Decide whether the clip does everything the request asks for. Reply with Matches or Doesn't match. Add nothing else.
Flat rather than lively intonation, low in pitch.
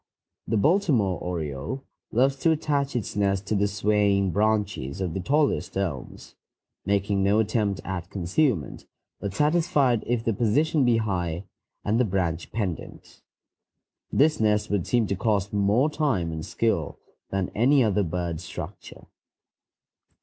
Doesn't match